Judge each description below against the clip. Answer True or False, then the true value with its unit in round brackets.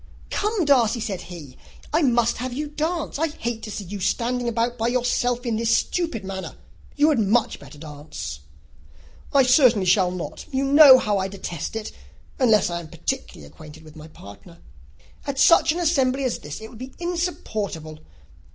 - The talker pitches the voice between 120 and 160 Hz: False (230 Hz)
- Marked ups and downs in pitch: True (6.7 semitones)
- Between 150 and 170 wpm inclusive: False (180 wpm)